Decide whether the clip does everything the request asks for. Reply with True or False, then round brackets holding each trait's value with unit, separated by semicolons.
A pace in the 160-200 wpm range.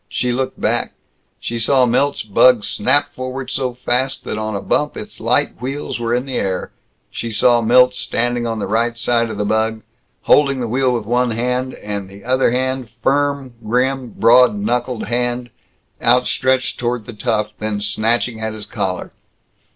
True (175 wpm)